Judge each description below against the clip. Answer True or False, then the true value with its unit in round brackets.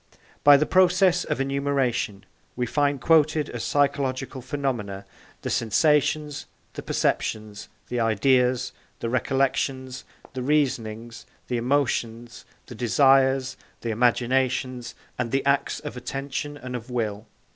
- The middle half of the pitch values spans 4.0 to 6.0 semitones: False (3.0 semitones)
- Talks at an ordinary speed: False (120 wpm)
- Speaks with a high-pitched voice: False (130 Hz)